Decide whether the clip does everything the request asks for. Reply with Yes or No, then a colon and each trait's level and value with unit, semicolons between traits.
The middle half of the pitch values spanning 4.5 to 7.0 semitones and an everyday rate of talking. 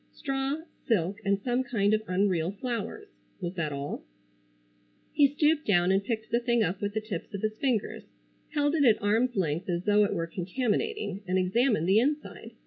Yes: average, 5.3 semitones; average, 185 wpm